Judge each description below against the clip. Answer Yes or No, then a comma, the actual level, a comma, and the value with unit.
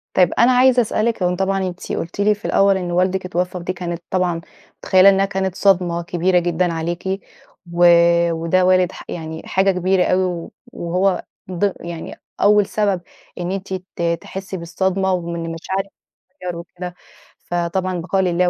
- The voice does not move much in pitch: Yes, narrow, 1.8 semitones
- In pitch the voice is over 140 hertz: Yes, medium, 185 Hz